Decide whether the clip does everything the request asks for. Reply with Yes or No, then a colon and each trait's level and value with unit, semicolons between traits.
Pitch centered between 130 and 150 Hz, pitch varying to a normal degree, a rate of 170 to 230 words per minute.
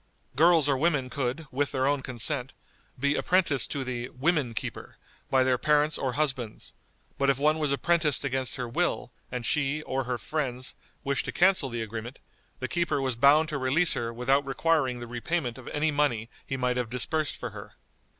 Yes: low, 135 Hz; average, 3.2 semitones; average, 190 wpm